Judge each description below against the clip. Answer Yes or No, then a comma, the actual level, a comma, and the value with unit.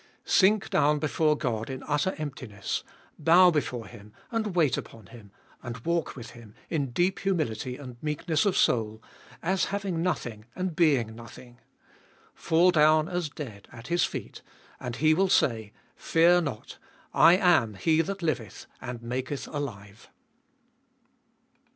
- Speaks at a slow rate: No, average, 145 wpm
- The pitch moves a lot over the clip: Yes, wide, 6.4 semitones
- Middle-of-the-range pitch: Yes, medium, 150 Hz